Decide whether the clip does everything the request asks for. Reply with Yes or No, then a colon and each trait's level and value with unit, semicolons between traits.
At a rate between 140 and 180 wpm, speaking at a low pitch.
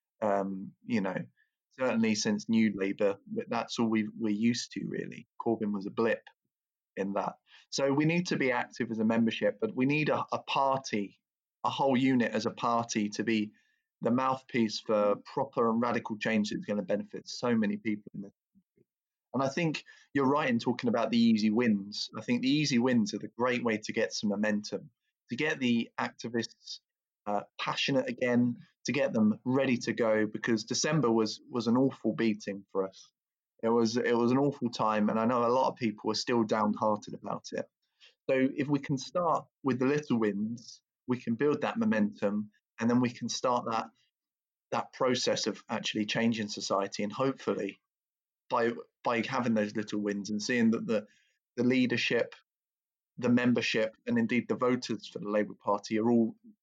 No: average, 190 wpm; low, 115 Hz